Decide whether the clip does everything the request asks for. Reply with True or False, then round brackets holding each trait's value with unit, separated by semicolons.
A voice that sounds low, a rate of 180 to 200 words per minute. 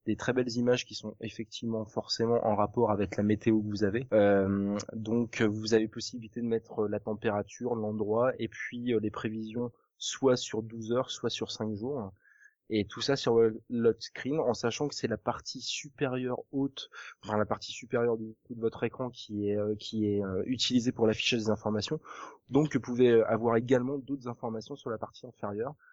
True (115 Hz; 185 wpm)